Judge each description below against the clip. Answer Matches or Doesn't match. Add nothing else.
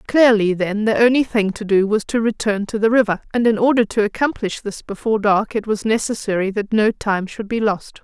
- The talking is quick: Matches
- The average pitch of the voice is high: Matches